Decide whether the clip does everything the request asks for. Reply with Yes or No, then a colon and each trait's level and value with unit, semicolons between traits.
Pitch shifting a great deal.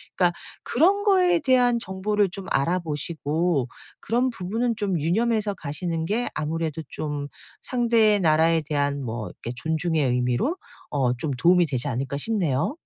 Yes: wide, 7.2 semitones